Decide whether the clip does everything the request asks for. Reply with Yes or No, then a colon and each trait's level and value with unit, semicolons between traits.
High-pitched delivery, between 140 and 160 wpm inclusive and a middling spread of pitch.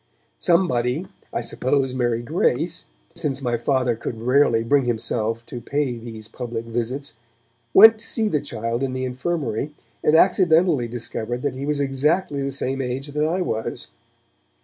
No: low, 130 Hz; average, 155 wpm; average, 3.8 semitones